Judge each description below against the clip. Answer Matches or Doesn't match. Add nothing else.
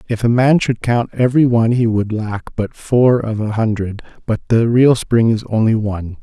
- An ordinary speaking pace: Doesn't match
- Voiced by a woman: Doesn't match